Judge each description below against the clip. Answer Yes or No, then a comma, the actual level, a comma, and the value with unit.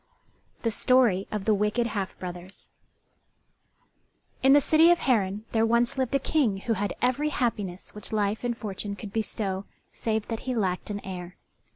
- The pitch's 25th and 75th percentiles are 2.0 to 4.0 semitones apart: Yes, average, 3.7 semitones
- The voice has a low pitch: No, high, 215 Hz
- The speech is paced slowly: No, average, 170 wpm